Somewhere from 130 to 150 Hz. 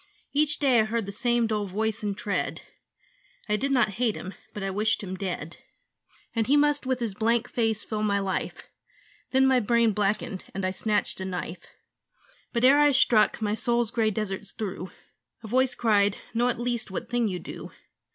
No: high, 220 Hz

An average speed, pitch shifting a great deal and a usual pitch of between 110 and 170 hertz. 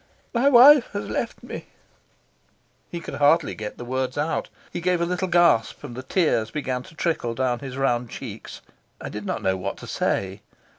Yes: average, 190 wpm; wide, 6.4 semitones; low, 135 Hz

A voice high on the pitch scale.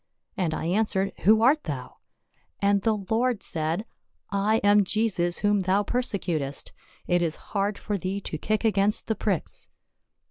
Yes: high, 200 Hz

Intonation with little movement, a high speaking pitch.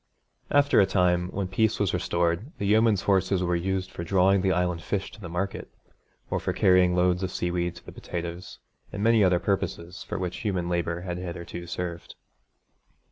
No: narrow, 1.9 semitones; very low, 90 Hz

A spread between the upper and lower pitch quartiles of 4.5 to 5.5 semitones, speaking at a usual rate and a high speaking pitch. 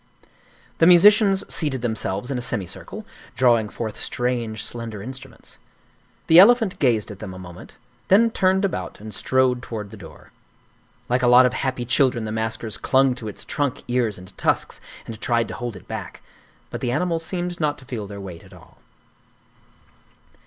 No: average, 5.1 semitones; average, 175 wpm; low, 125 Hz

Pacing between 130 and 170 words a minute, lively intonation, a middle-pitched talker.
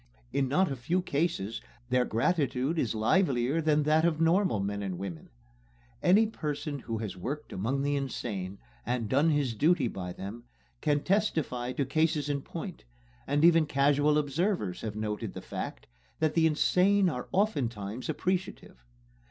Yes: average, 155 wpm; wide, 6.0 semitones; medium, 145 Hz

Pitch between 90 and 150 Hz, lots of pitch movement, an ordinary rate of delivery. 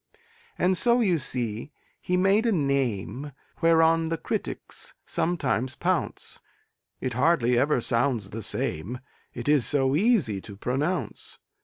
No: medium, 140 Hz; wide, 5.7 semitones; slow, 130 wpm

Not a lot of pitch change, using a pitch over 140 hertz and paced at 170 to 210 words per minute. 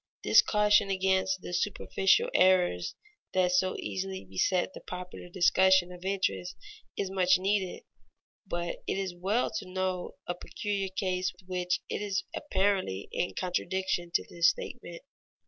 No: narrow, 1.5 semitones; medium, 185 Hz; slow, 135 wpm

